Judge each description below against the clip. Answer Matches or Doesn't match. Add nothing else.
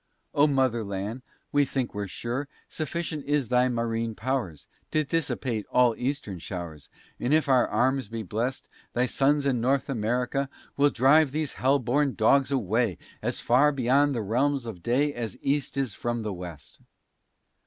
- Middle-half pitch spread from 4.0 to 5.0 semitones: Doesn't match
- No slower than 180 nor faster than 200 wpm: Doesn't match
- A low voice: Matches